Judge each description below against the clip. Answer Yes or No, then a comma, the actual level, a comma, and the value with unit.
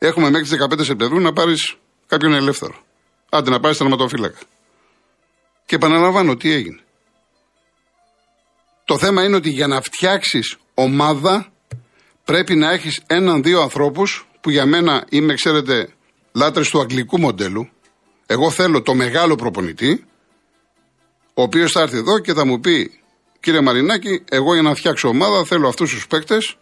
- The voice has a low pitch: No, medium, 155 Hz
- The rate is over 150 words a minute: No, average, 145 wpm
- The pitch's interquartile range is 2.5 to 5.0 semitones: Yes, average, 3.9 semitones